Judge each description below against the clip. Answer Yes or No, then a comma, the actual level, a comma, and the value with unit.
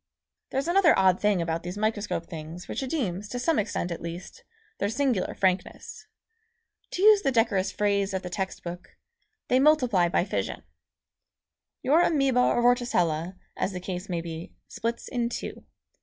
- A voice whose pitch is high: Yes, high, 205 Hz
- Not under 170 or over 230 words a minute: No, average, 160 wpm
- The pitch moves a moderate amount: No, wide, 5.7 semitones